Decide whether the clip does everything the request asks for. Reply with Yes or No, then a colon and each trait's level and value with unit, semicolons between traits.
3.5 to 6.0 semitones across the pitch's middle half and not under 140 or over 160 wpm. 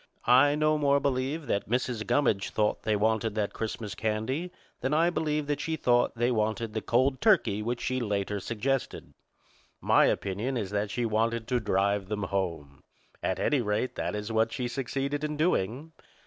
No: average, 4.7 semitones; average, 175 wpm